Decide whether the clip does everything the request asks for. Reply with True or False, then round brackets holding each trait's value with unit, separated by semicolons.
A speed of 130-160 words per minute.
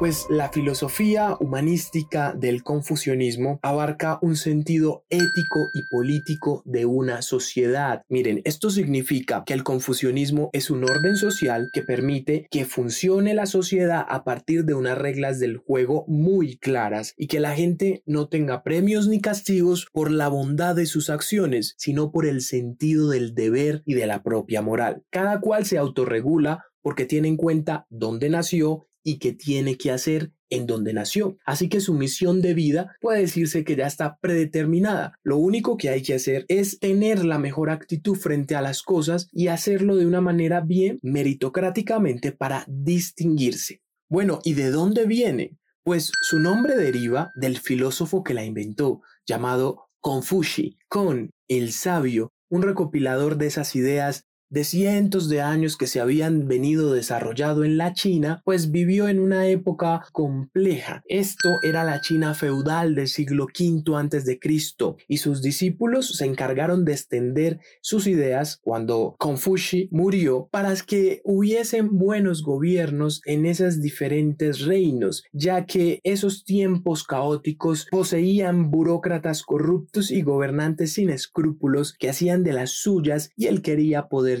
True (155 wpm)